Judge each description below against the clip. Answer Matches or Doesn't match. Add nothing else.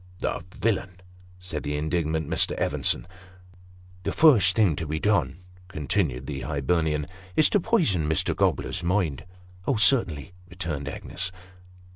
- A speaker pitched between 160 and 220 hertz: Doesn't match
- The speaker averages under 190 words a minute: Matches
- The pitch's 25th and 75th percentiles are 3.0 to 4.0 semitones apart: Matches